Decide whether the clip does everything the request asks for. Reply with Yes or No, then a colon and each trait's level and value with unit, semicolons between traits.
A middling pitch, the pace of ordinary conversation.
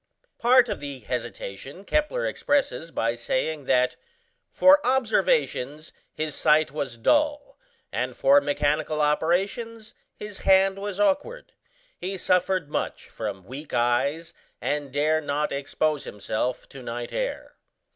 No: medium, 155 Hz; slow, 125 wpm